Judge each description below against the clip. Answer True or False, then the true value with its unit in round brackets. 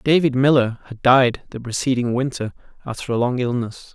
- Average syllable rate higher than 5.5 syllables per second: False (5.3 syllables/s)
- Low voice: True (125 Hz)